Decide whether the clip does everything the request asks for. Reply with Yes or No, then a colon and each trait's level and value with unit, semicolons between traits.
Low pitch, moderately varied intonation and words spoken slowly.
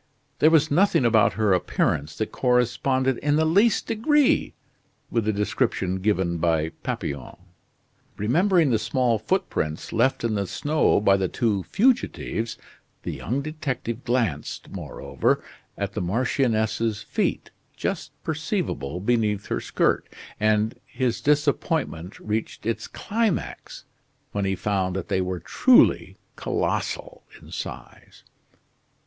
No: low, 115 Hz; wide, 6.6 semitones; slow, 125 wpm